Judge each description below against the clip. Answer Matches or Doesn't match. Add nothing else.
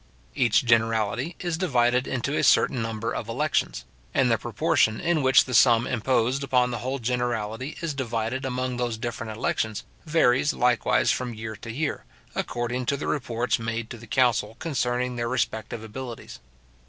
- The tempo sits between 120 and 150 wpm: Doesn't match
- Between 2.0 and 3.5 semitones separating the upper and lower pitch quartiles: Matches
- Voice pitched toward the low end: Matches